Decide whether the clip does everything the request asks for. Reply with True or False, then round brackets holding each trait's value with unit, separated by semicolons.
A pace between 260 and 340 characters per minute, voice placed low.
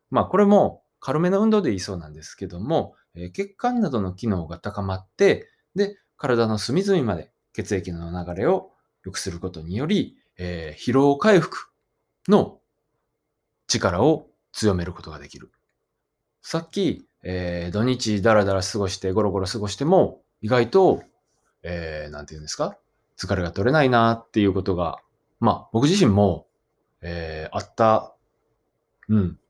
True (290 characters per minute; 100 Hz)